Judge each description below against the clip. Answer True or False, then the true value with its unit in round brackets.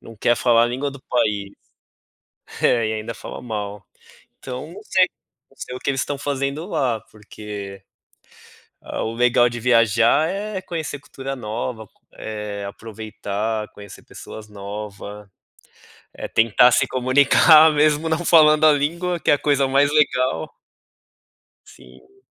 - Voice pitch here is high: False (125 Hz)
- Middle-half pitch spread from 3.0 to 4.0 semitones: False (5.3 semitones)